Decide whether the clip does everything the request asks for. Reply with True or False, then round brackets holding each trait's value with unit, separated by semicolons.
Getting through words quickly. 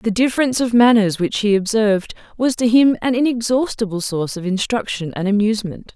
False (170 wpm)